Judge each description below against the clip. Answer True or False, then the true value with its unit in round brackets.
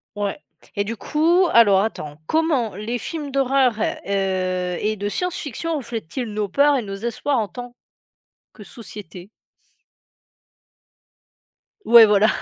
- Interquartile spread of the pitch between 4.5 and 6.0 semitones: True (5.3 semitones)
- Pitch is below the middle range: False (225 Hz)